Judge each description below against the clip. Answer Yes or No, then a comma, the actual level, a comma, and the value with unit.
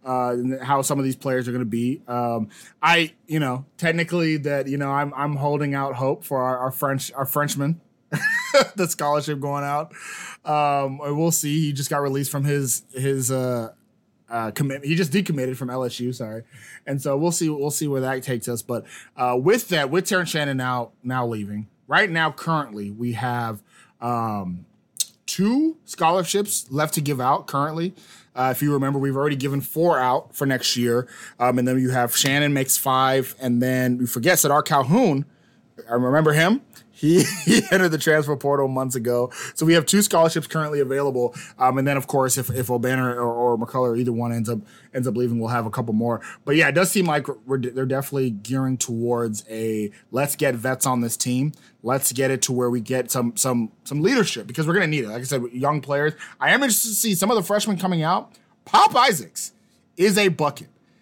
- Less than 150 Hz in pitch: Yes, low, 135 Hz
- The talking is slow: No, fast, 205 wpm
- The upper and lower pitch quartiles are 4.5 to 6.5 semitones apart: No, average, 3.7 semitones